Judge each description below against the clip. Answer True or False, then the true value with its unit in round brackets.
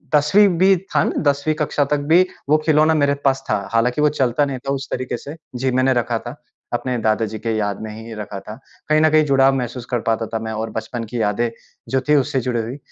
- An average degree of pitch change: True (4.2 semitones)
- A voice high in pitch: False (130 Hz)